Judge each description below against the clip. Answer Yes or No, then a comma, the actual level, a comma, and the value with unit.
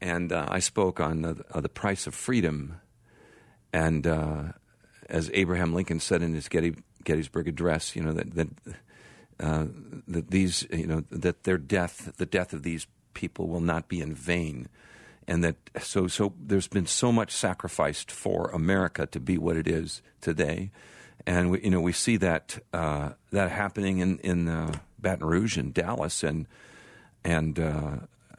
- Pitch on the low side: Yes, very low, 85 Hz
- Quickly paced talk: No, average, 170 wpm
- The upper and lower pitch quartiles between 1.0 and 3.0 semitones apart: Yes, narrow, 2.5 semitones